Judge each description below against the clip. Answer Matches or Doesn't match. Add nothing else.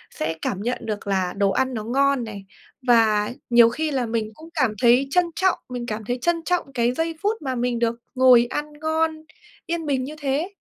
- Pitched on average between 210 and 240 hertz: Doesn't match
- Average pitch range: Matches